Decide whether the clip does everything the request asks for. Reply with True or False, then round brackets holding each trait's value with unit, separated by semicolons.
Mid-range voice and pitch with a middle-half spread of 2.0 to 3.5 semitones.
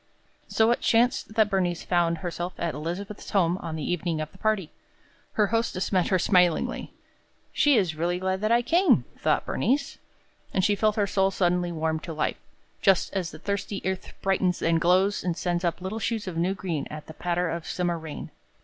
True (180 Hz; 2.9 semitones)